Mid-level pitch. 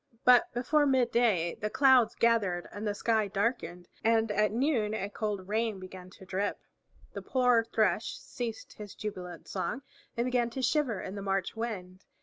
No: high, 215 Hz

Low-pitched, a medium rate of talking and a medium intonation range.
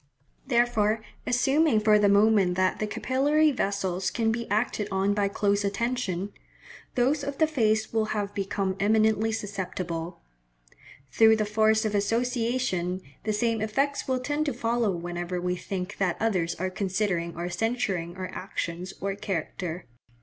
No: high, 210 Hz; average, 150 wpm; average, 3.6 semitones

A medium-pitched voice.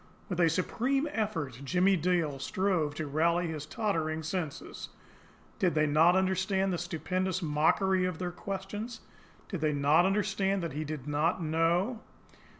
Yes: medium, 175 Hz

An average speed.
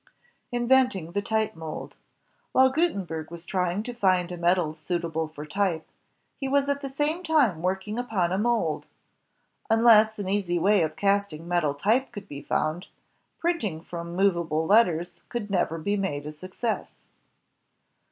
Yes: average, 150 wpm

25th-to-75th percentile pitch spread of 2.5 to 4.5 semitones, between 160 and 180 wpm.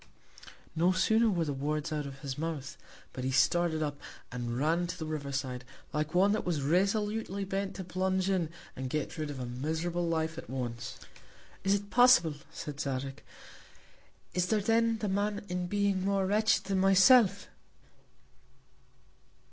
No: average, 5.2 semitones; average, 165 wpm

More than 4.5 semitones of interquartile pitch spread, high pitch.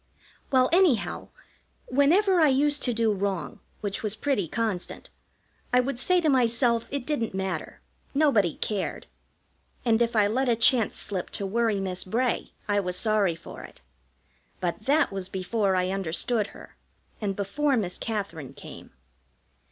Yes: average, 5.0 semitones; high, 220 Hz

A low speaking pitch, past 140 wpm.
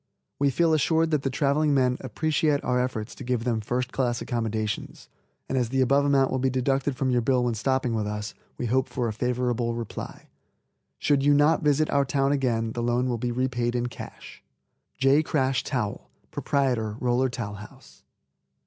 Yes: low, 125 Hz; average, 185 wpm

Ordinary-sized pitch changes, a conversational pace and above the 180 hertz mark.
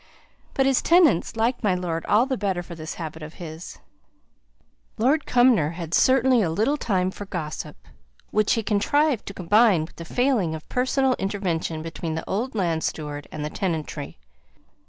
No: wide, 6.9 semitones; average, 170 wpm; high, 190 Hz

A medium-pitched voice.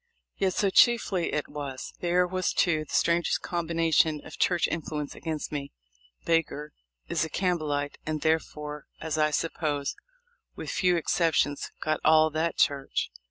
Yes: medium, 155 Hz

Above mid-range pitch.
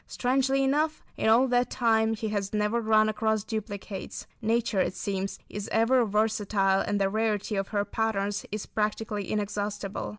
Yes: high, 215 Hz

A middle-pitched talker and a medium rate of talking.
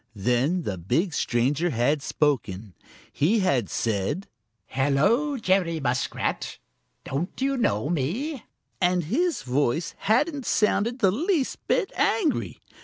No: medium, 170 Hz; slow, 115 wpm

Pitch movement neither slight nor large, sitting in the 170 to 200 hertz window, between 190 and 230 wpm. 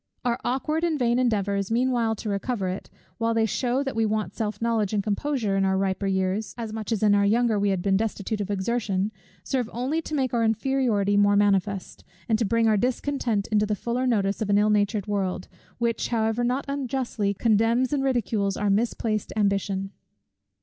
No: average, 3.2 semitones; high, 220 Hz; average, 195 wpm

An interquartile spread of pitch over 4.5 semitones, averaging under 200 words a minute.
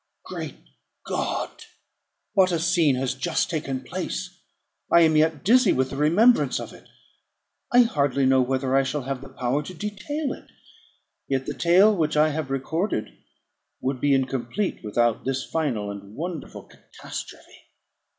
Yes: average, 5.1 semitones; average, 150 wpm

